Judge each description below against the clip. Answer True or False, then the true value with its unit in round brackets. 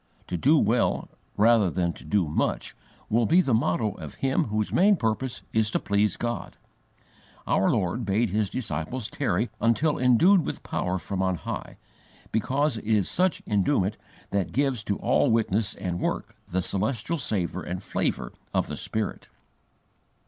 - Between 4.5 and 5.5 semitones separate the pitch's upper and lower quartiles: True (5.0 semitones)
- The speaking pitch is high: False (110 Hz)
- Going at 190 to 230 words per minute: False (160 wpm)